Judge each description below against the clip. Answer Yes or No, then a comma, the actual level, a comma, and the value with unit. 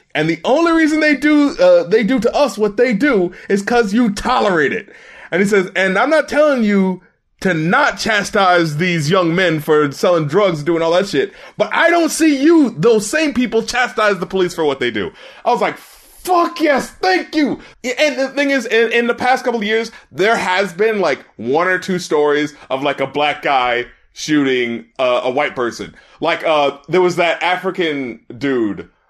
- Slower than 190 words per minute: No, fast, 205 wpm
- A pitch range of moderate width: No, wide, 7.2 semitones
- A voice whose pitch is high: Yes, high, 200 Hz